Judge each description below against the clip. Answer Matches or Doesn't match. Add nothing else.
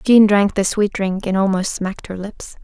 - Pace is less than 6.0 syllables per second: Matches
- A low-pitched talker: Doesn't match